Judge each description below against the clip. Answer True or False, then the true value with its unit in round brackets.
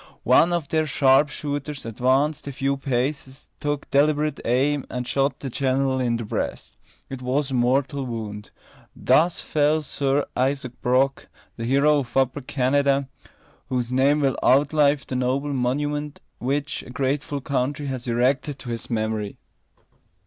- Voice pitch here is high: False (135 Hz)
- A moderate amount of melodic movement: False (2.3 semitones)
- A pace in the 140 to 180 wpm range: True (150 wpm)